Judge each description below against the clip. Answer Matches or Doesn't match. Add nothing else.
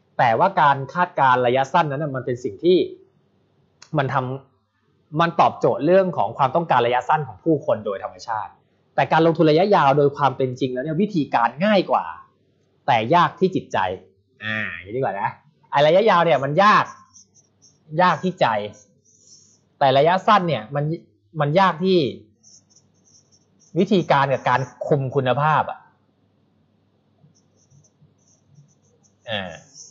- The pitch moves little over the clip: Doesn't match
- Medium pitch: Matches